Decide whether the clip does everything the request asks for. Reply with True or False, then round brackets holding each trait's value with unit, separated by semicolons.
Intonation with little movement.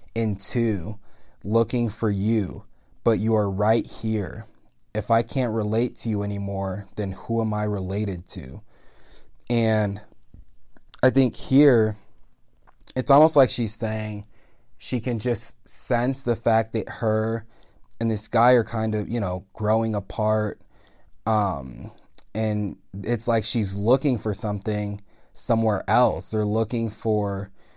True (1.8 semitones)